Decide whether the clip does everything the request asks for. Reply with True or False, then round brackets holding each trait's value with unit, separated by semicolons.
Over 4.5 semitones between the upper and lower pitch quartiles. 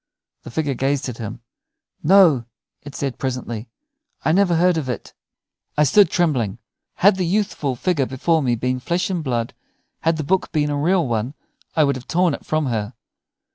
True (5.4 semitones)